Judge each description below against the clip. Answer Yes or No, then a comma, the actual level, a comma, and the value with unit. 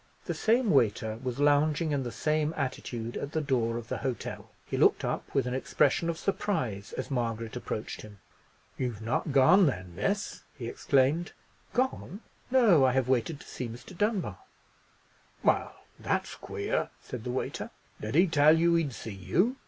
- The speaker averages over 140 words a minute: Yes, average, 170 wpm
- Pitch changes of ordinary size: No, wide, 6.1 semitones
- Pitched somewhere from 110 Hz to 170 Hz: Yes, low, 135 Hz